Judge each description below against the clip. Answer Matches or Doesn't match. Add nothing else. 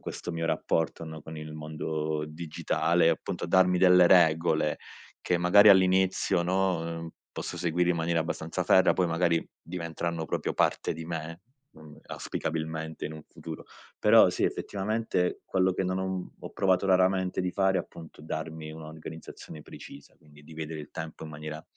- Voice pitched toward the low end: Matches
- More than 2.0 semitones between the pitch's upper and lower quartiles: Matches